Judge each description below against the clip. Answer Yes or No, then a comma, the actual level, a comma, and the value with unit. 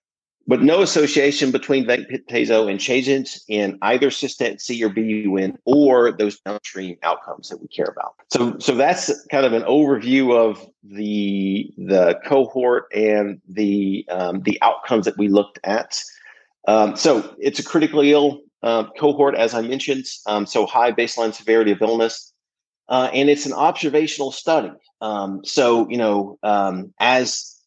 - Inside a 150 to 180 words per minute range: Yes, average, 155 wpm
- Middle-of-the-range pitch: No, low, 115 Hz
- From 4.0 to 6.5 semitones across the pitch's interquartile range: Yes, average, 5.0 semitones